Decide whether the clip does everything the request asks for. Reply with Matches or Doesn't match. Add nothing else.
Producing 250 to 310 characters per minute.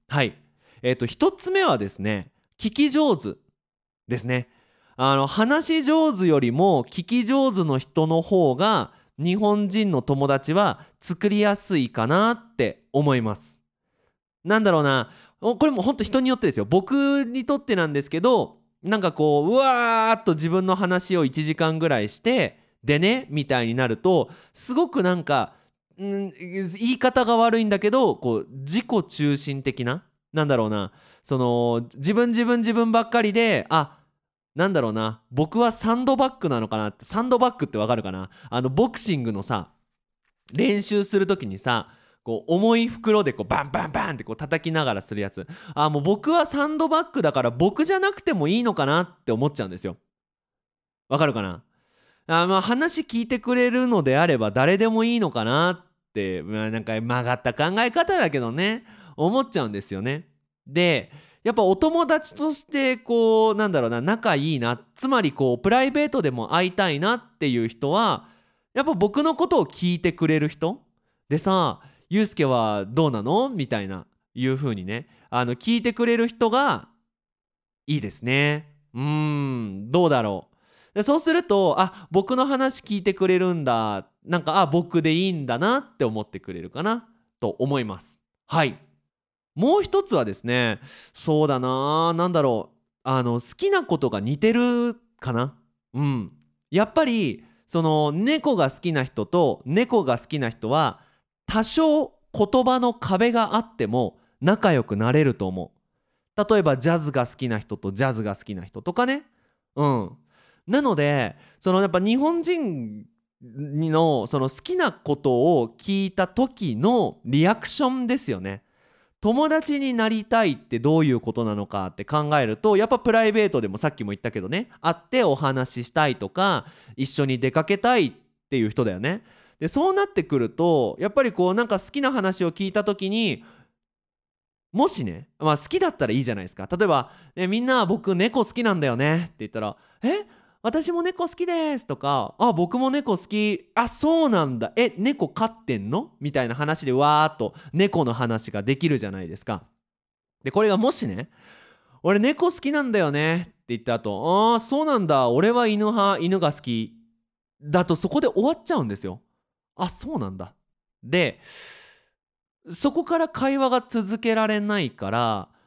Doesn't match